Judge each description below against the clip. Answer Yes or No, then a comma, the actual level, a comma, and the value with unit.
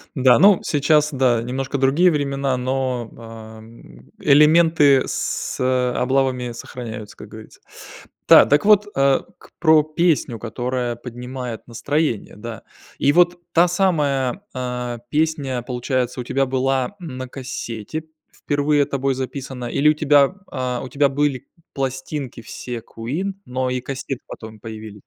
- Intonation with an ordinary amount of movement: Yes, average, 3.0 semitones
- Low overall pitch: Yes, low, 130 Hz